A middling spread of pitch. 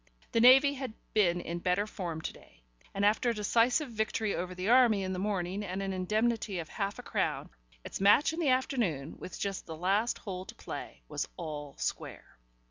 Yes: average, 4.3 semitones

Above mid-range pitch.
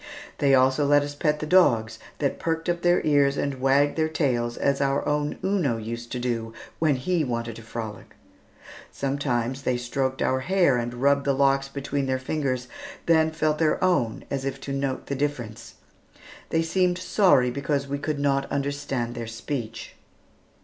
No: medium, 140 Hz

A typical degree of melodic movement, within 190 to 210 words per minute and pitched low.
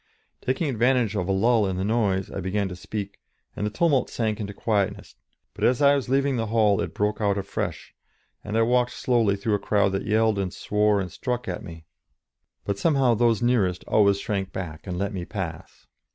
Yes: average, 3.4 semitones; fast, 205 wpm; low, 105 Hz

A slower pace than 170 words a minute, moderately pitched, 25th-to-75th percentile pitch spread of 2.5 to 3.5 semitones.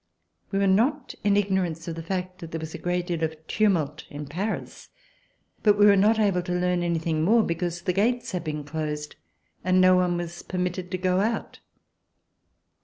No: average, 195 wpm; medium, 180 Hz; average, 3.0 semitones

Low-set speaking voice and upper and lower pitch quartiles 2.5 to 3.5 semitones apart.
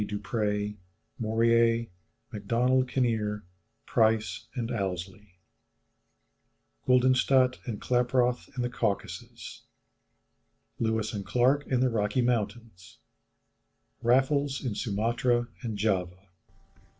Yes: low, 115 Hz; average, 3.1 semitones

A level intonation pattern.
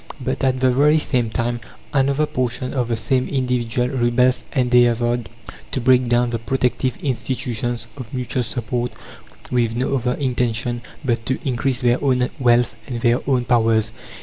Yes: narrow, 1.5 semitones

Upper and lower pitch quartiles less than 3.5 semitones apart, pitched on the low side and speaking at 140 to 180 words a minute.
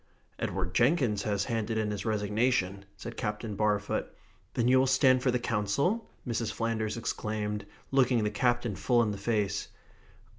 Yes: average, 2.9 semitones; low, 110 Hz; average, 155 wpm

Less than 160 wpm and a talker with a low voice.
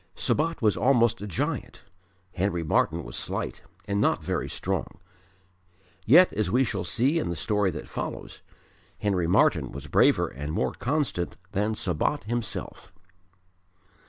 Yes: average, 140 wpm; low, 105 Hz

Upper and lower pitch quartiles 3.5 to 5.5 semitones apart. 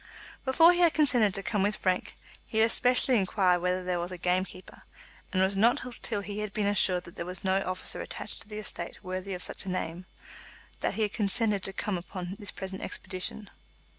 No: narrow, 2.5 semitones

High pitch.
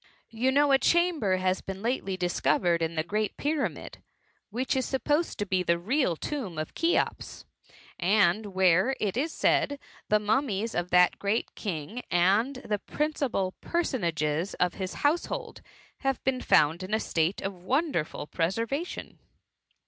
Yes: high, 205 Hz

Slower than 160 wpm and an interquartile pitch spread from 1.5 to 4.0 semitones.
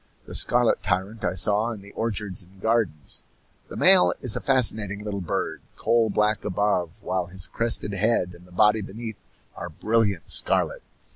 No: average, 165 wpm; average, 3.3 semitones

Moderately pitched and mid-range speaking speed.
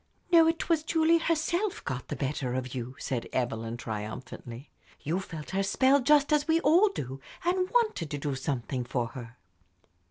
Yes: medium, 150 Hz; average, 170 wpm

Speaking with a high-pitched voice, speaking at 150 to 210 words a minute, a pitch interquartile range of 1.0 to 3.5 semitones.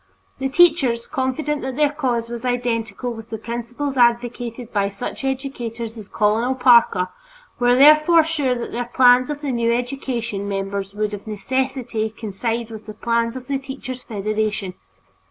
Yes: high, 240 Hz; average, 155 wpm; average, 3.0 semitones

